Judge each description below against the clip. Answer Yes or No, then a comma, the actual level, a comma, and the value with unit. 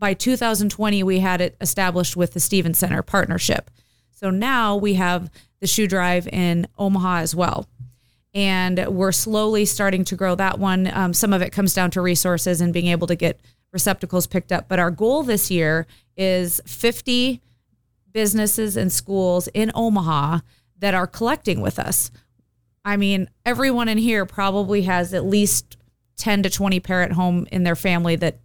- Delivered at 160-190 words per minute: Yes, average, 170 wpm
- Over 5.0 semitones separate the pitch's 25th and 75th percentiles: No, average, 2.7 semitones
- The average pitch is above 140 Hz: Yes, medium, 185 Hz